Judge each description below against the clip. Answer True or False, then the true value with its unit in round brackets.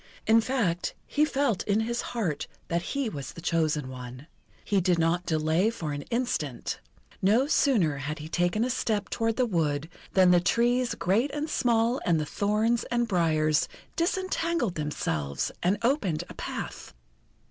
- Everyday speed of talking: True (160 wpm)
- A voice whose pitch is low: False (190 Hz)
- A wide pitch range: True (7.1 semitones)